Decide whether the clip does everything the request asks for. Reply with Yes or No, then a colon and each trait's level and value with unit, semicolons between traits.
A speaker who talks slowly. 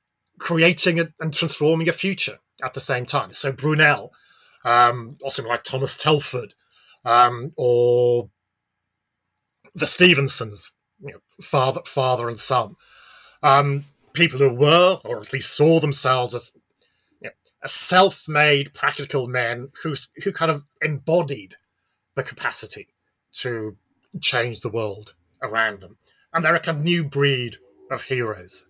Yes: slow, 130 wpm